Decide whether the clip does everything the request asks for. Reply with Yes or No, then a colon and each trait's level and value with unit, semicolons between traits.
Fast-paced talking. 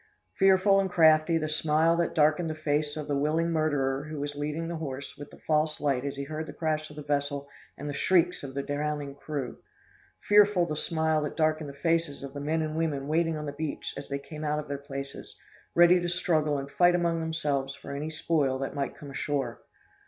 Yes: fast, 220 wpm